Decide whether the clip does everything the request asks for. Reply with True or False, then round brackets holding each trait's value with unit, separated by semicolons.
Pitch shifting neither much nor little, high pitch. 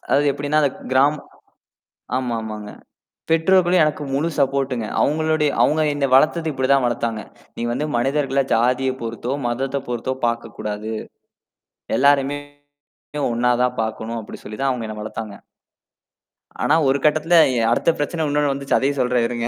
False (3.7 semitones; 135 Hz)